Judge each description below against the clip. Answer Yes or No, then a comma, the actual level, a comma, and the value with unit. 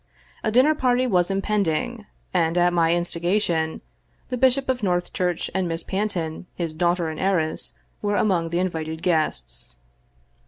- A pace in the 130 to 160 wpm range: Yes, average, 150 wpm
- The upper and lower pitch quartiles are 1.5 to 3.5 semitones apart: No, average, 4.1 semitones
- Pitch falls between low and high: Yes, medium, 175 Hz